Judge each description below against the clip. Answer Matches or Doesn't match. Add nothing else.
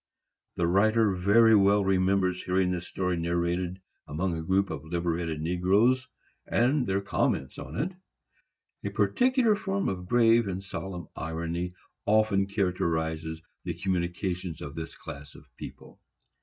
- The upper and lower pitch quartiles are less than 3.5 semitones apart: Matches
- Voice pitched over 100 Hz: Doesn't match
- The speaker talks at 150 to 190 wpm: Doesn't match